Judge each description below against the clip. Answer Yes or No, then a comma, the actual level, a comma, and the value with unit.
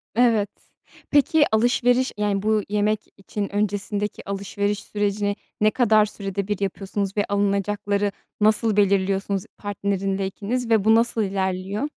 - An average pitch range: No, narrow, 1.4 semitones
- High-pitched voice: Yes, high, 205 Hz